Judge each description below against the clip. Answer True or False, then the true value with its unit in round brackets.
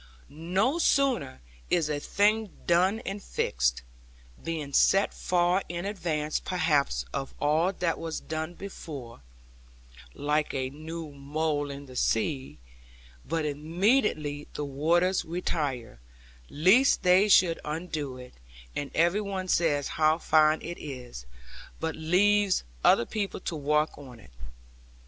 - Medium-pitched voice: True (160 Hz)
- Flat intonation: False (4.0 semitones)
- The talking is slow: True (125 wpm)